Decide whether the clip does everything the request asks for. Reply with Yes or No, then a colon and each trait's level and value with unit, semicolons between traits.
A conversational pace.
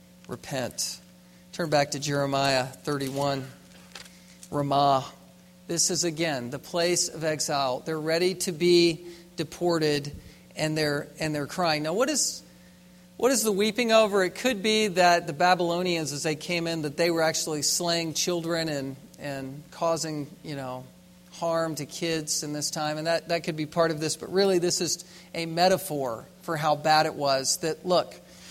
Yes: average, 170 wpm